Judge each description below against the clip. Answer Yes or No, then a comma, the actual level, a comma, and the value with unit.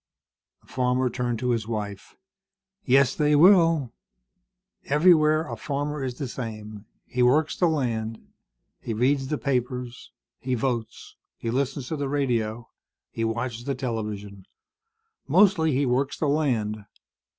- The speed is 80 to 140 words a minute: Yes, slow, 135 wpm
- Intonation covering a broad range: No, average, 4.1 semitones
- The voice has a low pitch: Yes, low, 125 Hz